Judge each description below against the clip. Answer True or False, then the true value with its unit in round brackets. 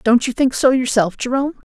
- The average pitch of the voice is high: True (250 Hz)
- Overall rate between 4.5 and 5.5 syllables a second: False (6.1 syllables/s)